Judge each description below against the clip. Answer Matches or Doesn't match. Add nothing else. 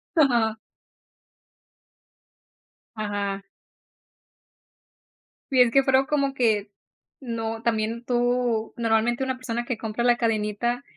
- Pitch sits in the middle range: Doesn't match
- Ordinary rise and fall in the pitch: Doesn't match